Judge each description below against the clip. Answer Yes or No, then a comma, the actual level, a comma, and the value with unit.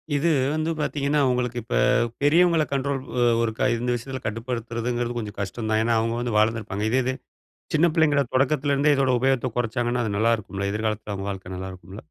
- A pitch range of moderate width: Yes, average, 3.9 semitones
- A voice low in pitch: Yes, low, 120 Hz